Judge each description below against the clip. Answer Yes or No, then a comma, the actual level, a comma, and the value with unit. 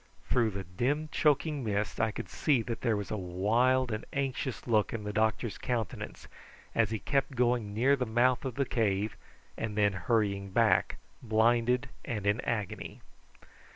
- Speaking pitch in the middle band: No, low, 115 Hz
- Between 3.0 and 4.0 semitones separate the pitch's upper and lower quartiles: Yes, average, 3.3 semitones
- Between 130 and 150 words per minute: No, average, 165 wpm